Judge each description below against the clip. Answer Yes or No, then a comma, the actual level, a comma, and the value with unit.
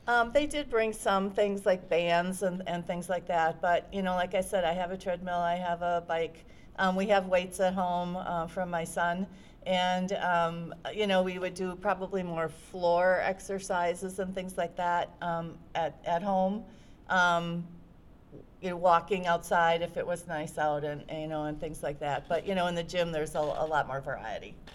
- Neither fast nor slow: No, fast, 210 wpm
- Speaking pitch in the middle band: Yes, medium, 175 Hz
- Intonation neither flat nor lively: No, narrow, 2.0 semitones